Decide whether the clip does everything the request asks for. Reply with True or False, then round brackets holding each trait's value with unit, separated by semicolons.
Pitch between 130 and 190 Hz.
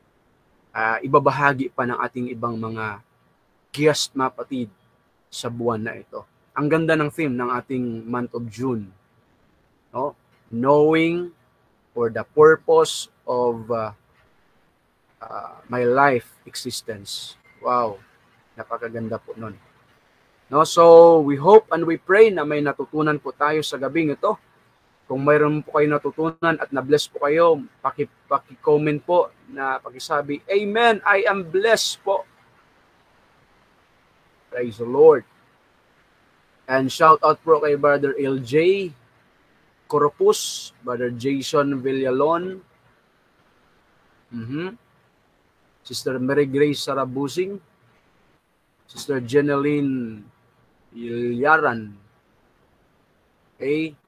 True (140 Hz)